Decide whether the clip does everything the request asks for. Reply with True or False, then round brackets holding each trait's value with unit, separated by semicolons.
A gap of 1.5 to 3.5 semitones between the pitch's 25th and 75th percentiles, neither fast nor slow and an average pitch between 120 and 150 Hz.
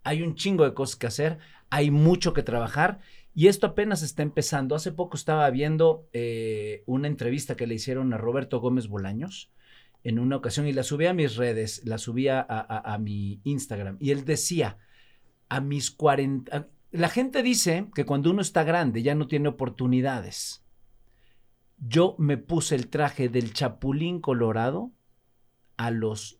False (4.5 semitones; 170 wpm; 135 Hz)